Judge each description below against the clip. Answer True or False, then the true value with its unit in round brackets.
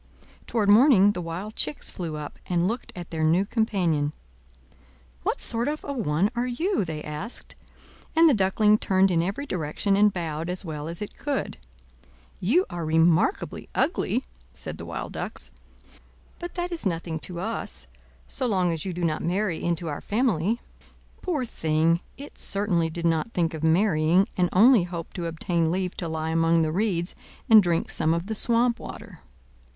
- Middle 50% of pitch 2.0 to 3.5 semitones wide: False (4.9 semitones)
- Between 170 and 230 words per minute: True (175 wpm)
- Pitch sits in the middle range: True (180 Hz)